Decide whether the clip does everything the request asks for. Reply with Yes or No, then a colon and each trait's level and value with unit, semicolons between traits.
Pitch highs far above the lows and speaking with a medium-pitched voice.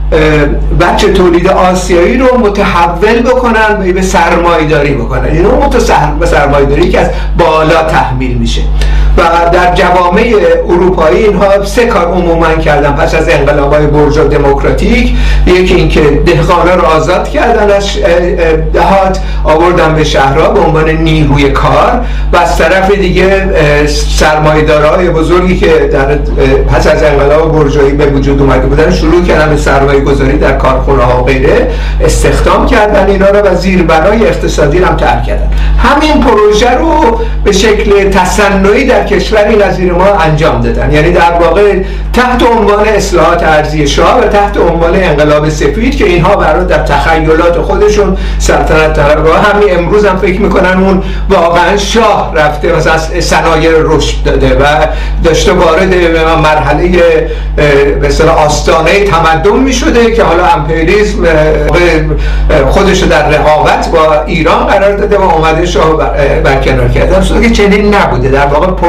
No: average, 4.6 semitones; medium, 170 Hz